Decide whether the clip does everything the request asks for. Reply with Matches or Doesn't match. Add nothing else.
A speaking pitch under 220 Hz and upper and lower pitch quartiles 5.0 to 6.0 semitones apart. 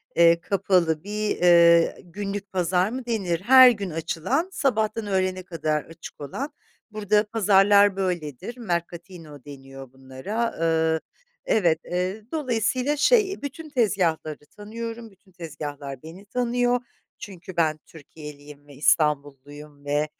Matches